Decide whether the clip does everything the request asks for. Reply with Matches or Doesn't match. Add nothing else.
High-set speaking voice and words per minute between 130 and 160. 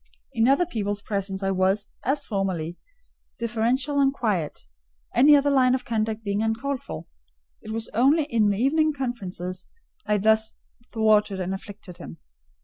Matches